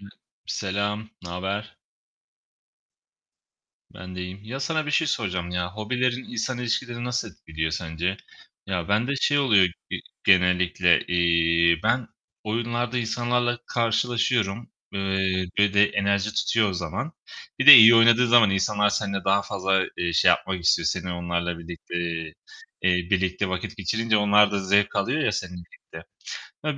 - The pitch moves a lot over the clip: No, average, 4.3 semitones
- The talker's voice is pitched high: No, low, 100 Hz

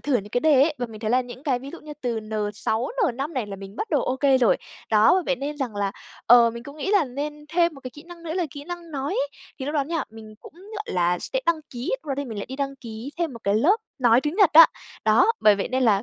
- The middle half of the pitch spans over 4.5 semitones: Yes, average, 5.1 semitones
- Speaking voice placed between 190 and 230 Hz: No, very high, 265 Hz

